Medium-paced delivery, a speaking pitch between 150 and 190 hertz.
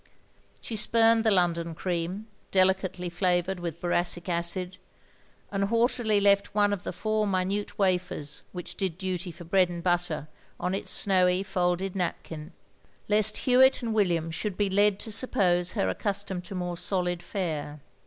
Yes: average, 155 wpm; medium, 185 Hz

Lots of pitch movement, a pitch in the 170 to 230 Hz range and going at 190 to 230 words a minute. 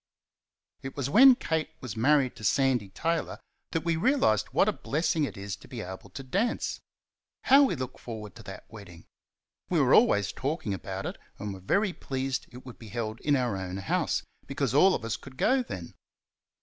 No: wide, 7.5 semitones; low, 130 Hz; average, 195 wpm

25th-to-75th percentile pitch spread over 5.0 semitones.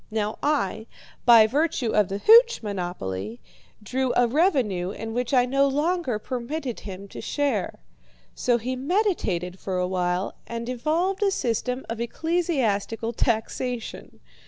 Yes: wide, 5.6 semitones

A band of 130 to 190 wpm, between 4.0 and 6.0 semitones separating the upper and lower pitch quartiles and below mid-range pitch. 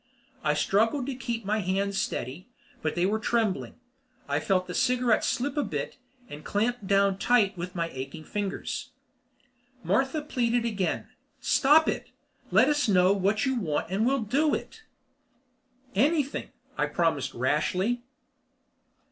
No: average, 145 wpm; average, 5.1 semitones; high, 215 Hz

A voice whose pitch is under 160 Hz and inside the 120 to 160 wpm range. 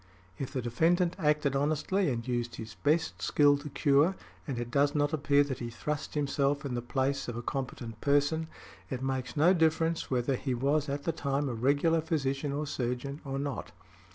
No: medium, 140 Hz; average, 190 wpm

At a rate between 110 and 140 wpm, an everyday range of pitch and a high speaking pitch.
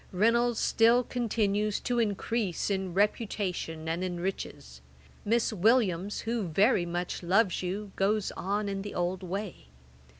Yes: slow, 135 wpm; average, 3.6 semitones; high, 200 Hz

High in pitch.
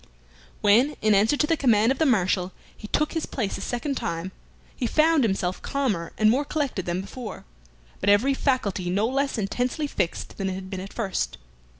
Yes: high, 220 Hz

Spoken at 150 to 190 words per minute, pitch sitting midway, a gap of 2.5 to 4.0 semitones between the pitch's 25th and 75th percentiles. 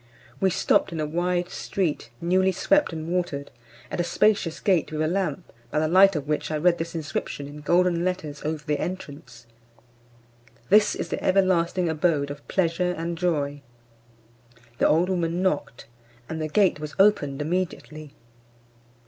Yes: average, 160 wpm; medium, 170 Hz; average, 3.2 semitones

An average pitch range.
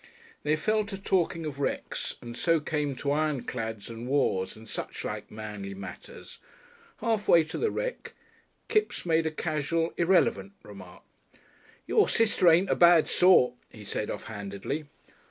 No: wide, 7.7 semitones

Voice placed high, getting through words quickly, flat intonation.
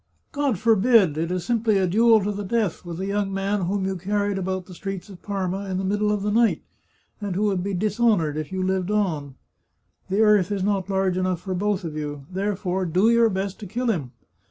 Yes: high, 195 Hz; fast, 225 wpm; narrow, 2.2 semitones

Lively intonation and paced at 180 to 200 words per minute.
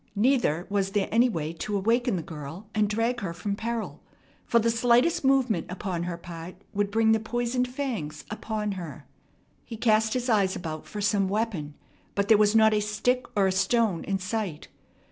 No: average, 3.7 semitones; average, 185 wpm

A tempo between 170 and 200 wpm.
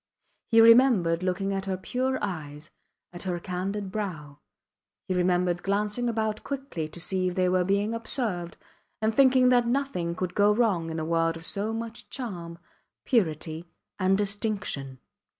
No: average, 155 wpm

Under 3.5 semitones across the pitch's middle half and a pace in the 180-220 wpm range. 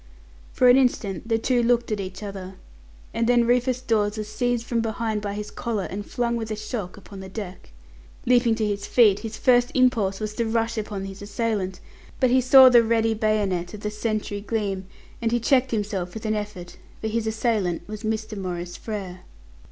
Yes: narrow, 2.6 semitones; average, 200 wpm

